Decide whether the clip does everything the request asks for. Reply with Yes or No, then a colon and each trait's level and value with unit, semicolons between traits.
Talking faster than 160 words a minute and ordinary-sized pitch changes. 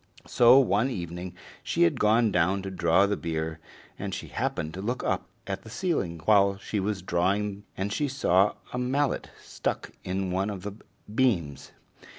Yes: average, 170 wpm; average, 3.5 semitones